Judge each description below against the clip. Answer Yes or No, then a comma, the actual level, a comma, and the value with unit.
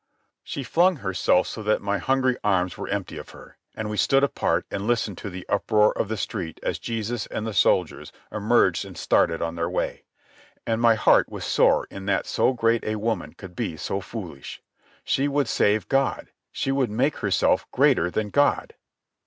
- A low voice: Yes, low, 110 Hz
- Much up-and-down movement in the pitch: No, average, 3.8 semitones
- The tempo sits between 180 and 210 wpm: Yes, average, 190 wpm